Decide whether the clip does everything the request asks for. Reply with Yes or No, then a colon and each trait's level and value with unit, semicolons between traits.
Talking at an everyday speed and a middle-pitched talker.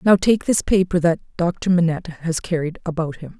Yes: average, 195 wpm; medium, 170 Hz